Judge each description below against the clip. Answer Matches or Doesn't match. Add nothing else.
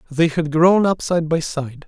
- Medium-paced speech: Doesn't match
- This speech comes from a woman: Doesn't match